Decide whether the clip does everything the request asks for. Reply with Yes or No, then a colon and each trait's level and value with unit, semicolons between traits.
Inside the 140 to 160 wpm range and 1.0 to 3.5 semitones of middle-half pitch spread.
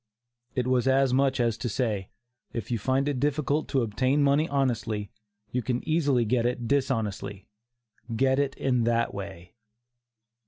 Yes: average, 155 wpm; average, 3.2 semitones